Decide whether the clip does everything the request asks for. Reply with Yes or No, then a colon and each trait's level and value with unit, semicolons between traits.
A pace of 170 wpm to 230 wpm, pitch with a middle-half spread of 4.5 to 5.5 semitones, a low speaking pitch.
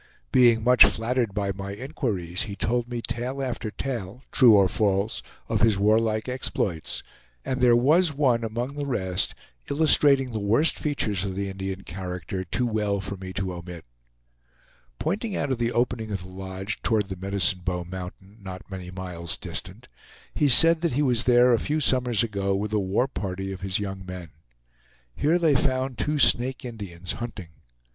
Yes: average, 175 wpm; average, 4.8 semitones; low, 110 Hz